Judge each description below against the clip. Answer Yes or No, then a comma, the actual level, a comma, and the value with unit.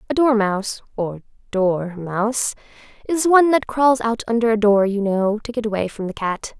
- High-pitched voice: Yes, high, 220 Hz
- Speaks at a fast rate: No, average, 180 wpm